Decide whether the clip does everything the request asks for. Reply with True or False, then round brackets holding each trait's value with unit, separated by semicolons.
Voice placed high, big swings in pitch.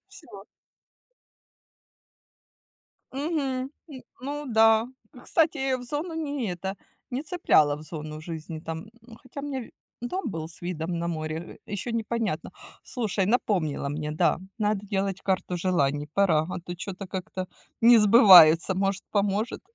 True (195 Hz; 6.6 semitones)